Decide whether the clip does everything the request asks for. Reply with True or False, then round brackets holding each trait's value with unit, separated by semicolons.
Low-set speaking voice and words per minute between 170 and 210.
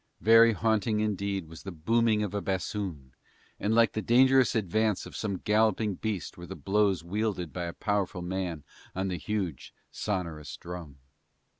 False (100 Hz; 160 wpm)